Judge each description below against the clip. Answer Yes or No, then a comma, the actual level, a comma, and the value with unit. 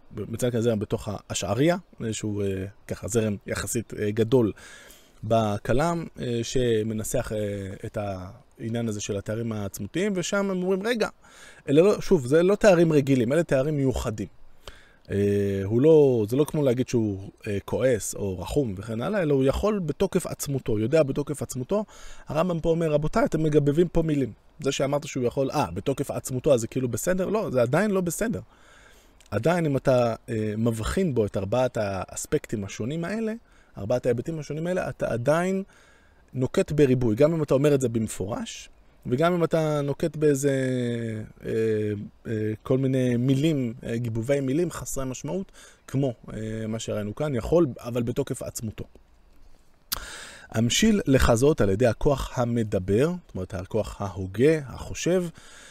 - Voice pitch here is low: Yes, low, 125 Hz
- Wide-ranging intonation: Yes, wide, 5.7 semitones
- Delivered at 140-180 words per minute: Yes, fast, 150 wpm